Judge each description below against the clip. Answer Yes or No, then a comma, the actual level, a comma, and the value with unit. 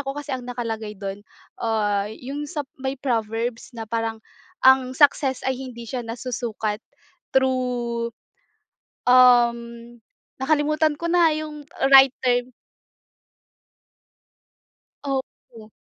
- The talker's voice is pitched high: Yes, very high, 250 Hz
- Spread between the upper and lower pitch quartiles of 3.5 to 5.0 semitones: No, average, 3.0 semitones